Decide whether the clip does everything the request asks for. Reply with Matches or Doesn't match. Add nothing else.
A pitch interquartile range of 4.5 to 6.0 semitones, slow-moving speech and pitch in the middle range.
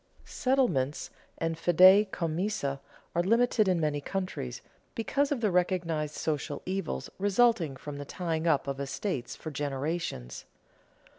Matches